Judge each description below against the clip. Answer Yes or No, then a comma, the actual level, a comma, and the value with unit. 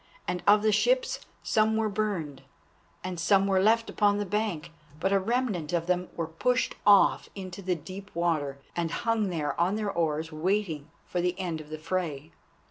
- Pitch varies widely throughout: No, average, 4.0 semitones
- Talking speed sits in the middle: Yes, average, 185 wpm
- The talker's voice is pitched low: No, medium, 185 Hz